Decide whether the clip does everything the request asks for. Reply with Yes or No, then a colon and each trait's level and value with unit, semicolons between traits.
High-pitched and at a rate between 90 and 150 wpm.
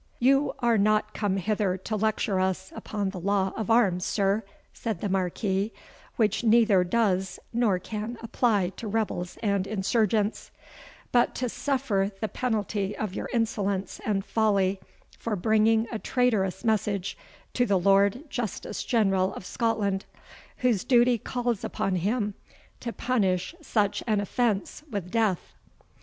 Yes: high, 210 Hz; average, 140 wpm